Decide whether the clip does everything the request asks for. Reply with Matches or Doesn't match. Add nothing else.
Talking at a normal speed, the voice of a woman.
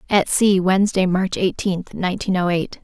Matches